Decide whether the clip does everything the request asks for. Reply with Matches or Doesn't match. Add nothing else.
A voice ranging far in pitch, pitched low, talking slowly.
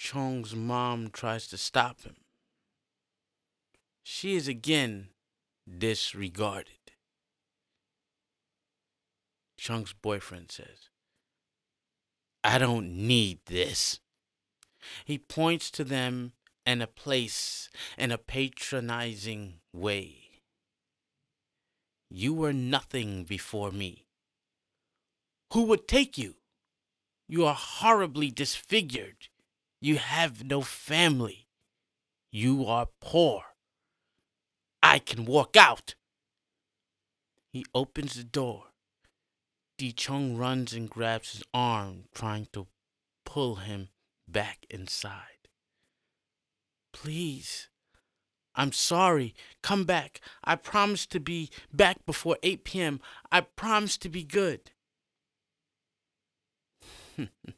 Matches